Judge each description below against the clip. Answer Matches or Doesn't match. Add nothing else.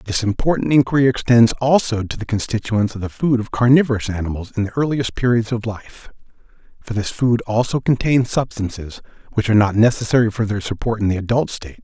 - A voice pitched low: Matches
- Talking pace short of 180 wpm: Doesn't match